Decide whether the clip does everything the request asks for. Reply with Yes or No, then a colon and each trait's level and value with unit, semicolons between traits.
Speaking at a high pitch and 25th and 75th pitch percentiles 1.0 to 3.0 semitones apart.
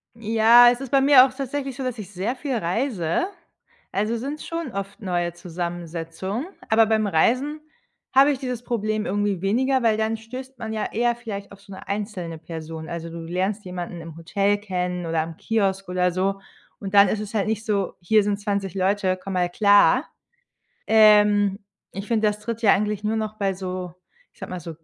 No: high, 205 Hz; average, 3.8 semitones